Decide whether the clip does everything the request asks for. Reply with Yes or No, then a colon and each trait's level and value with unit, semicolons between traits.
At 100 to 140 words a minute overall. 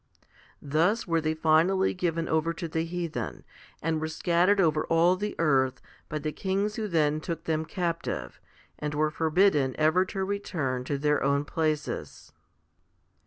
No: average, 160 wpm